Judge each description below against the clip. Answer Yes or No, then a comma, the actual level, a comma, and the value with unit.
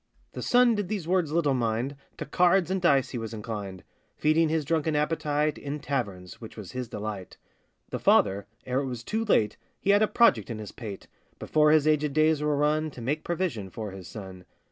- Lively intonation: Yes, wide, 6.3 semitones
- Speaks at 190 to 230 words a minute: Yes, fast, 205 wpm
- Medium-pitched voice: Yes, medium, 145 Hz